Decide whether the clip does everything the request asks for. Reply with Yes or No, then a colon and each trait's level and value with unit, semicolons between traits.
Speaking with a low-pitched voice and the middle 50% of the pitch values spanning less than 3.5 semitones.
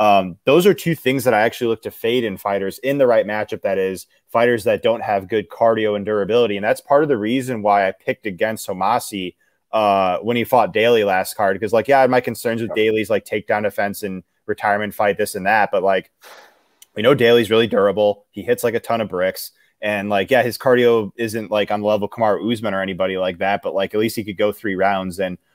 Yes: low, 105 Hz; average, 3.0 semitones